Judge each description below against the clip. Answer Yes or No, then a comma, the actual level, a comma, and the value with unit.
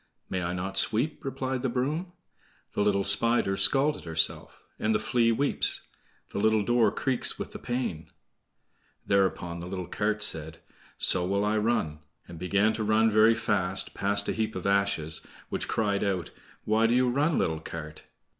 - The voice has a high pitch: No, low, 105 Hz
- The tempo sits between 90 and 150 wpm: No, average, 170 wpm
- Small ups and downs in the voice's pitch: No, average, 3.8 semitones